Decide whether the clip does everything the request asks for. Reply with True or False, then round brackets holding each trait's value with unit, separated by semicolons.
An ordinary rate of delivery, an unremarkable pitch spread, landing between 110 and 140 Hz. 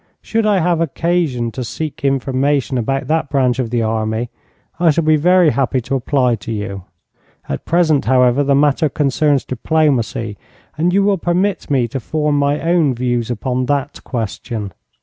True (170 wpm; 4.4 semitones; 135 Hz)